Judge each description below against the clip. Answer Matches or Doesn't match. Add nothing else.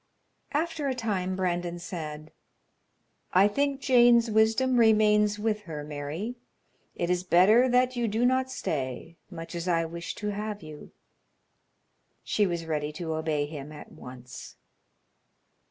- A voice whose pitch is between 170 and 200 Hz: Matches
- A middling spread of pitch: Doesn't match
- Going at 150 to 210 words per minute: Doesn't match